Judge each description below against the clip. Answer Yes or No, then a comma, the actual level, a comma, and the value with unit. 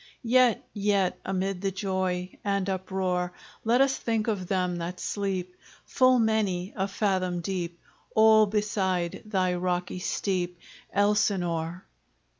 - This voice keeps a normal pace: No, slow, 120 wpm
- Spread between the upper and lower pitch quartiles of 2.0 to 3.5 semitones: Yes, narrow, 2.5 semitones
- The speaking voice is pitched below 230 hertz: Yes, high, 190 Hz